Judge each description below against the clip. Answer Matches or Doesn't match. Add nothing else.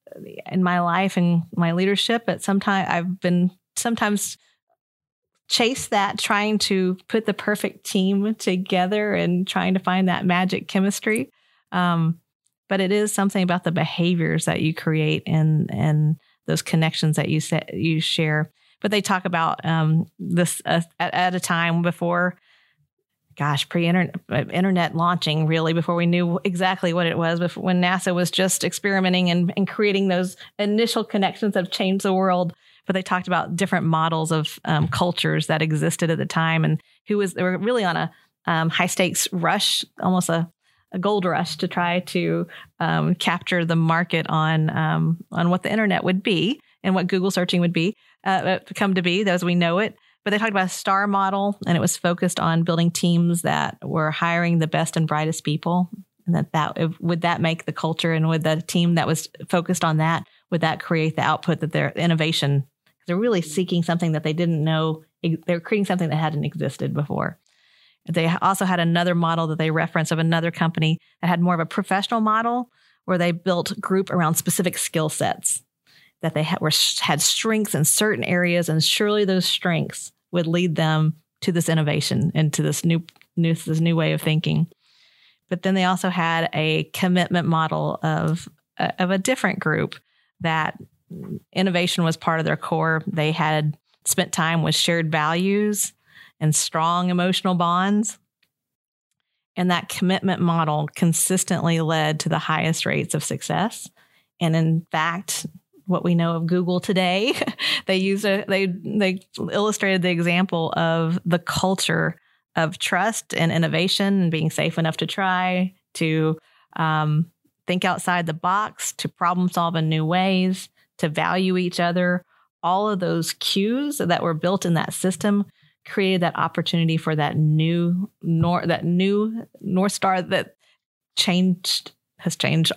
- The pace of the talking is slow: Doesn't match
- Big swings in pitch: Doesn't match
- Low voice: Doesn't match